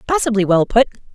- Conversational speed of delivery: Yes, average, 155 wpm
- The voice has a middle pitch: No, high, 220 Hz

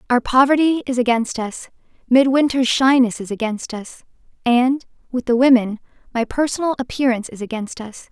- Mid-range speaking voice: No, very high, 250 Hz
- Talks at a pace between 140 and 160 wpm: Yes, average, 150 wpm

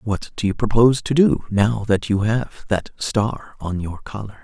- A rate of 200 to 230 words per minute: Yes, fast, 205 wpm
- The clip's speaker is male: Yes, male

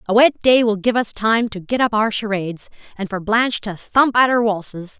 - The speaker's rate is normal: No, fast, 240 wpm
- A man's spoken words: No, female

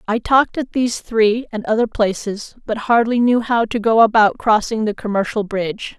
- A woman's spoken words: Yes, female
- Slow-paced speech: No, average, 190 wpm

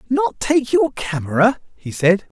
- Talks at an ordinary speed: Yes, average, 150 wpm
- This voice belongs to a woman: No, male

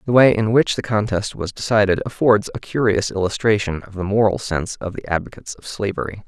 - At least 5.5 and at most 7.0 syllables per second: Yes, 6.0 syllables/s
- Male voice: Yes, male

